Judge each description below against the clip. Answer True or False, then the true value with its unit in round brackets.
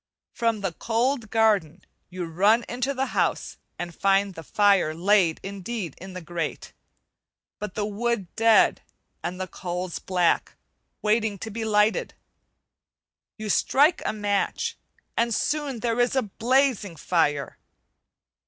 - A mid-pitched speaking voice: False (205 Hz)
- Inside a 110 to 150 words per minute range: True (135 wpm)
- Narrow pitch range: False (4.1 semitones)